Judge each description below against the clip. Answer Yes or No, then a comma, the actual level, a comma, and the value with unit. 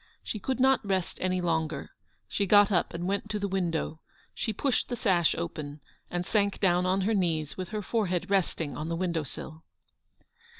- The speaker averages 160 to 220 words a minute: Yes, average, 185 wpm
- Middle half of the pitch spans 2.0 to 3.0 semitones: No, average, 3.4 semitones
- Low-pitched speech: No, medium, 185 Hz